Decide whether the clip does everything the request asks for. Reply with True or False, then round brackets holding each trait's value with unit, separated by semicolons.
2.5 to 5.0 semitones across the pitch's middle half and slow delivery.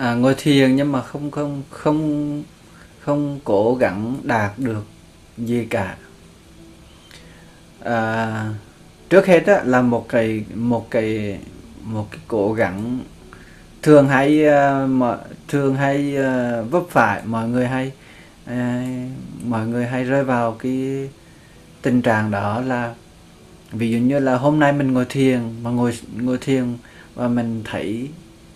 True (3.4 semitones; 130 wpm)